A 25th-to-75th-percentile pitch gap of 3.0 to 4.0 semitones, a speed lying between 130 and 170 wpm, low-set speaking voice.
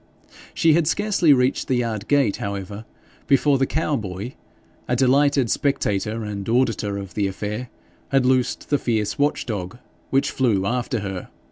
No: average, 5.0 semitones; average, 155 wpm; low, 120 Hz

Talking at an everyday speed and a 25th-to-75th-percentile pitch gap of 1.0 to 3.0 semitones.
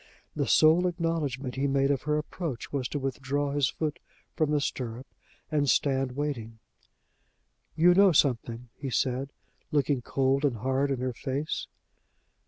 Yes: average, 150 wpm; narrow, 2.6 semitones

